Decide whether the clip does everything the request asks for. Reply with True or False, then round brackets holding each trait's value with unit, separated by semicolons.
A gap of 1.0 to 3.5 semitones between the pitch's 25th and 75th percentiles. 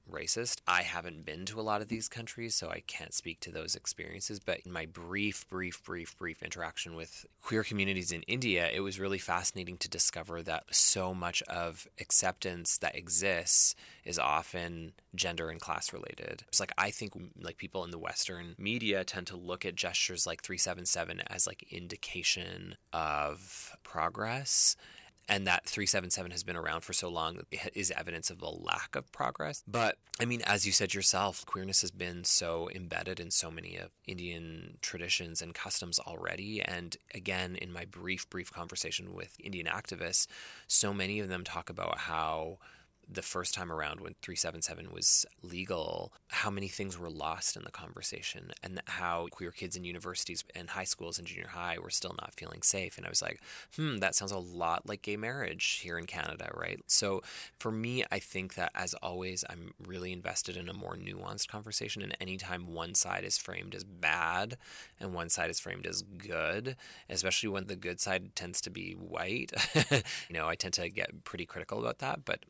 True (2.4 semitones)